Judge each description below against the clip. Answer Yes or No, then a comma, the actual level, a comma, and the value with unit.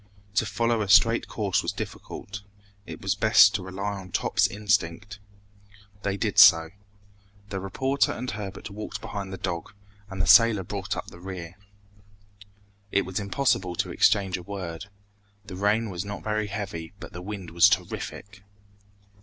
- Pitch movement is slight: Yes, narrow, 2.2 semitones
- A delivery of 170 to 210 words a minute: No, average, 160 wpm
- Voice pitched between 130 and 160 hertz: No, low, 100 Hz